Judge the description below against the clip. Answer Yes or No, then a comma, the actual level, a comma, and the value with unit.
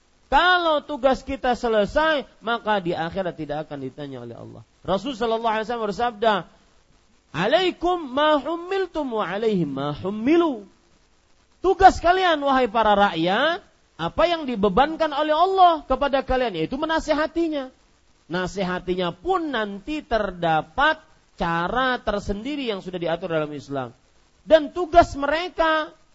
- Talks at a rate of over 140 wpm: No, average, 105 wpm